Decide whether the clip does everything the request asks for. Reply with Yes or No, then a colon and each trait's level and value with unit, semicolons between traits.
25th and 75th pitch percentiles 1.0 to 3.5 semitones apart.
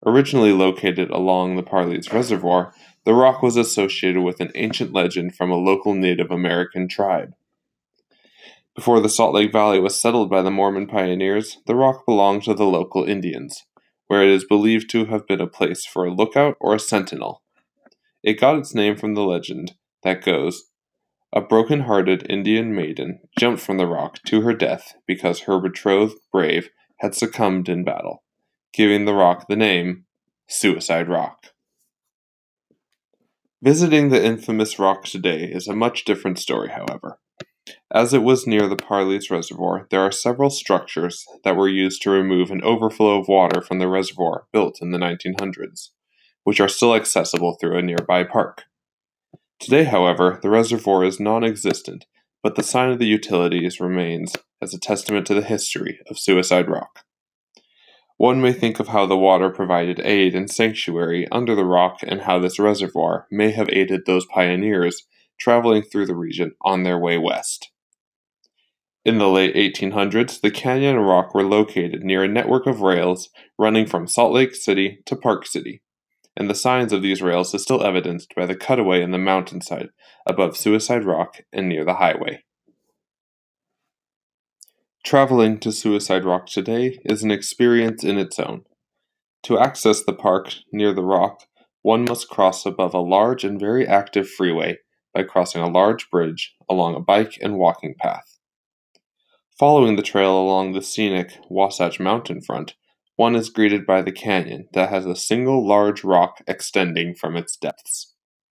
Yes: average, 3.0 semitones